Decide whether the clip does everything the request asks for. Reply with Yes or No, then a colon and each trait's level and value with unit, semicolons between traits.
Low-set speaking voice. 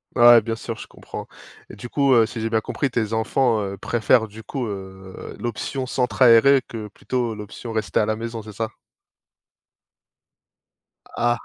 Yes: low, 115 Hz